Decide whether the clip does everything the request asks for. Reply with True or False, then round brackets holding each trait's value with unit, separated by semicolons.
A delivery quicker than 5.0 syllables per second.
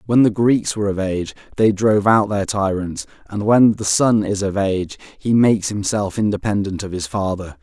True (5.2 syllables/s)